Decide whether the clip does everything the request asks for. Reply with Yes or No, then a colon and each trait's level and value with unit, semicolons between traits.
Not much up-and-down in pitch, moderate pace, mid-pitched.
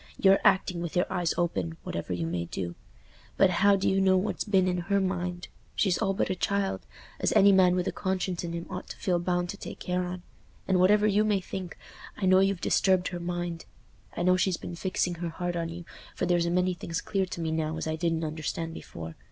No: narrow, 2.0 semitones; fast, 230 wpm; medium, 180 Hz